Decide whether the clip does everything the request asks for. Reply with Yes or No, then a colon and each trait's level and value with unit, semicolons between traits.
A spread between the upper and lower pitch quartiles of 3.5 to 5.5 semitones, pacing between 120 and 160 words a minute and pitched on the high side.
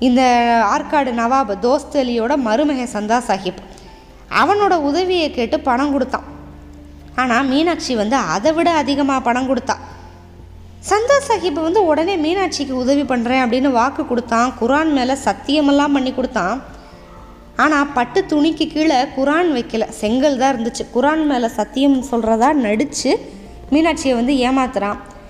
Yes: average, 4.9 semitones; average, 125 wpm; very high, 260 Hz